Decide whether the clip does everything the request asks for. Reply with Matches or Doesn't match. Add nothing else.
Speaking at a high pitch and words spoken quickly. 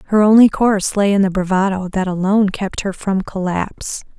Doesn't match